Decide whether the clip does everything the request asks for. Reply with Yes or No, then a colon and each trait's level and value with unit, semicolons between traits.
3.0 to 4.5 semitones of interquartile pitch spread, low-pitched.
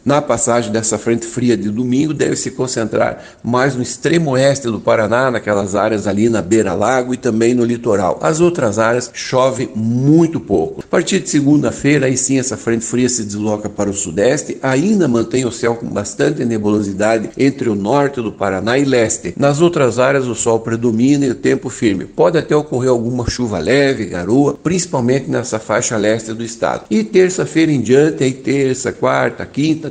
Yes: average, 3.5 semitones; low, 125 Hz